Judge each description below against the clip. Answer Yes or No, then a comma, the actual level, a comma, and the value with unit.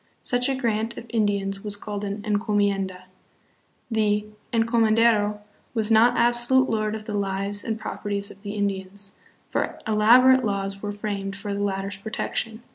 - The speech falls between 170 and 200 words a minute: No, average, 155 wpm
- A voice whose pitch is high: Yes, high, 210 Hz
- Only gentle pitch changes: Yes, narrow, 2.0 semitones